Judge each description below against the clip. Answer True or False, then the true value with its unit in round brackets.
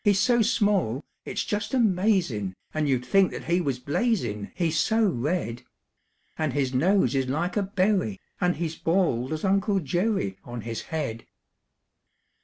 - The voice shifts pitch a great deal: True (7.3 semitones)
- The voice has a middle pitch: True (170 Hz)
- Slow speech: False (165 wpm)